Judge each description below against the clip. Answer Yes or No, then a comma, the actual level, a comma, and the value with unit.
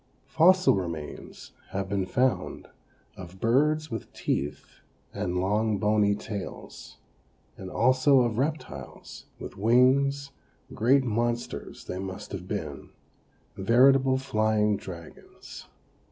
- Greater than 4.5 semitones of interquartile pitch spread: Yes, wide, 5.4 semitones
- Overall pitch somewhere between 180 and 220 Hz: No, low, 115 Hz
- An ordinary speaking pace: No, slow, 105 wpm